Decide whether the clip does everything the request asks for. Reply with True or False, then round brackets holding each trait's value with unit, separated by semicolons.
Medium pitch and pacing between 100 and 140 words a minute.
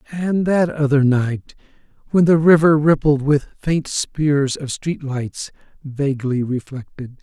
True (145 Hz; 135 wpm)